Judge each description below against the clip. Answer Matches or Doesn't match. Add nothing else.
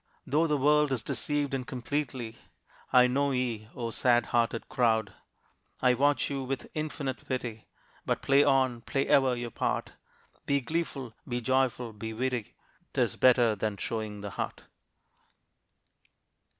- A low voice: Matches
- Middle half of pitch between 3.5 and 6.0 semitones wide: Doesn't match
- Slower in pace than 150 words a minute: Matches